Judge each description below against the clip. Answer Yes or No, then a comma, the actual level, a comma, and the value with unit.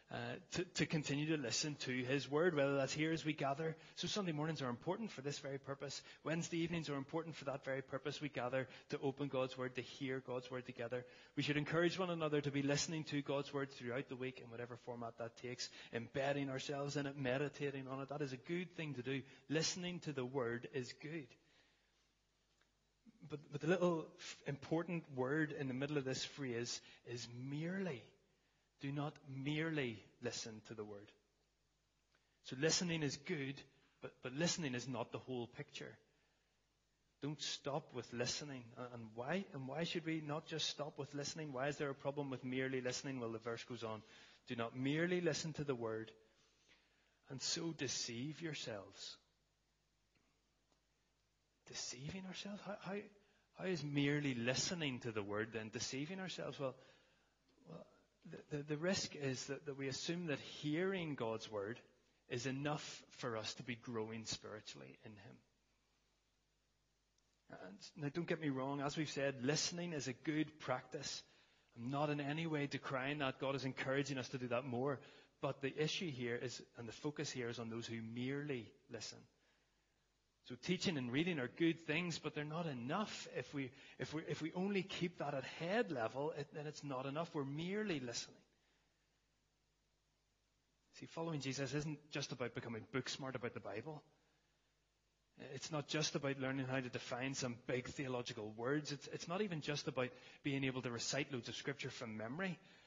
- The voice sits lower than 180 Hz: Yes, medium, 140 Hz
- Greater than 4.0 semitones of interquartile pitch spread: No, average, 3.4 semitones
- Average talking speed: Yes, average, 180 wpm